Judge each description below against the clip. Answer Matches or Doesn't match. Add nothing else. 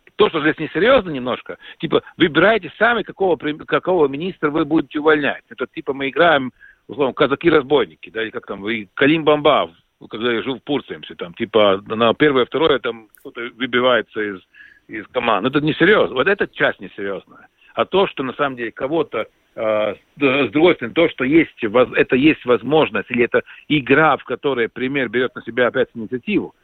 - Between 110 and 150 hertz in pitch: Matches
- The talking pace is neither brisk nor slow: Doesn't match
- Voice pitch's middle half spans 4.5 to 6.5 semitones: Matches